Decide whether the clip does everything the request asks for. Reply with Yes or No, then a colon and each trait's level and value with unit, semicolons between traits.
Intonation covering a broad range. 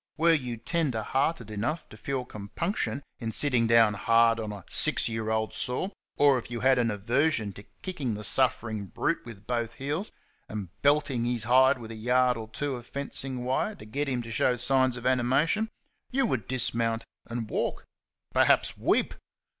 No: average, 3.3 semitones